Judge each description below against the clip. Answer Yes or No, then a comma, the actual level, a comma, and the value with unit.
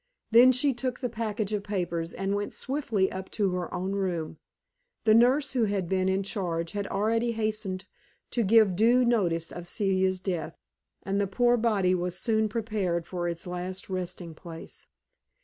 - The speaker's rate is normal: Yes, average, 170 wpm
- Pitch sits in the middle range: No, high, 195 Hz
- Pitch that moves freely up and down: No, average, 3.8 semitones